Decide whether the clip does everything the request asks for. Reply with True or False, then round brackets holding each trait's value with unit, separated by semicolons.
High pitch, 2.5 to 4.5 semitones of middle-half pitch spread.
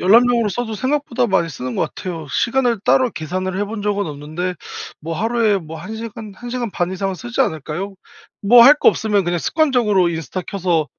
False (200 Hz; 5.4 semitones)